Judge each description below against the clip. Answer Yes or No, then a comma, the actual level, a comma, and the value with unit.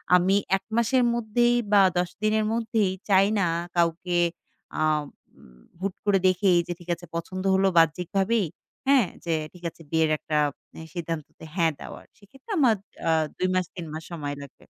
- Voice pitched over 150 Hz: Yes, medium, 185 Hz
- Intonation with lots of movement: No, average, 4.0 semitones